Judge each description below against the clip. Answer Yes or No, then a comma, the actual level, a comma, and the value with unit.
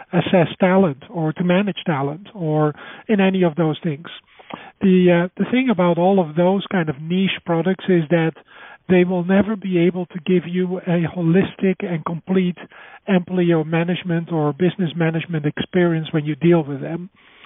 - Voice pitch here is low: No, medium, 180 Hz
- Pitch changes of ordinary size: No, narrow, 2.3 semitones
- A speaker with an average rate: Yes, average, 170 wpm